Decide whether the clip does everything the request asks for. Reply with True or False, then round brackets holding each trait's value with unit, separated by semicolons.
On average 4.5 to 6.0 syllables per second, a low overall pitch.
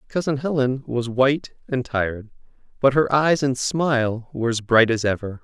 True (5.0 syllables/s; 130 Hz)